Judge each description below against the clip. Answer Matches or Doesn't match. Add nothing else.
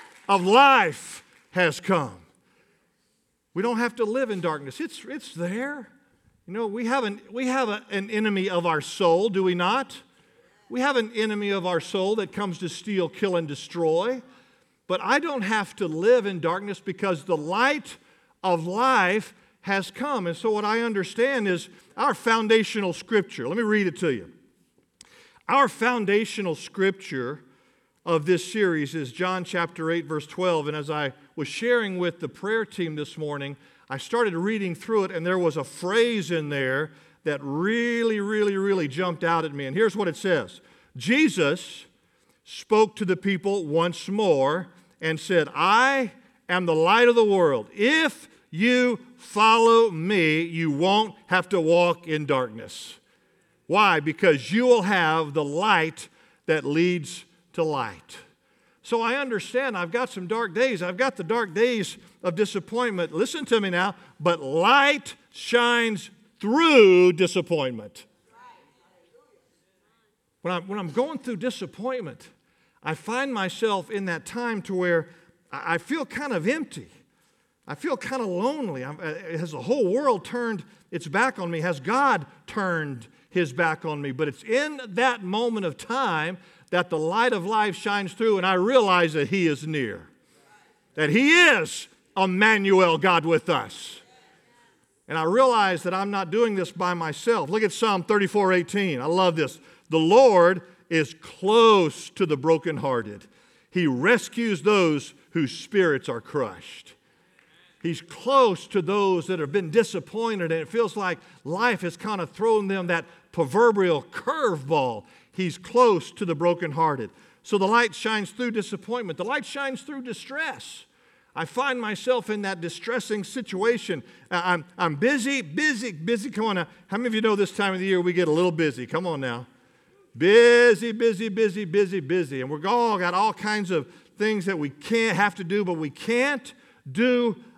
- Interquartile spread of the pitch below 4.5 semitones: Doesn't match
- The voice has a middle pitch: Doesn't match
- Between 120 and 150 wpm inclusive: Doesn't match